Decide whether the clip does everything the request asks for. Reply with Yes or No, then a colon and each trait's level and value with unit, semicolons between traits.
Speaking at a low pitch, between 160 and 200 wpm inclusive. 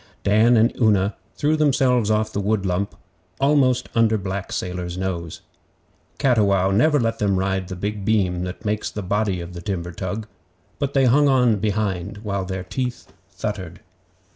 Yes: low, 105 Hz; average, 165 wpm